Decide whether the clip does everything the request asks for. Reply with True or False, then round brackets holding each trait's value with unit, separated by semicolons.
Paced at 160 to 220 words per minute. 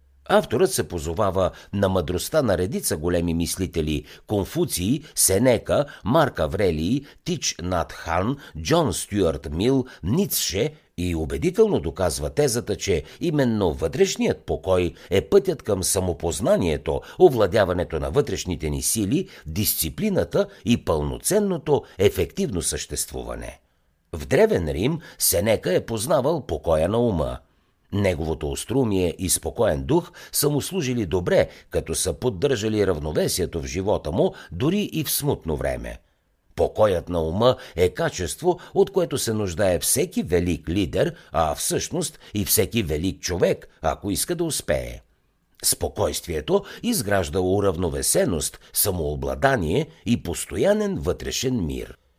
False (115 wpm)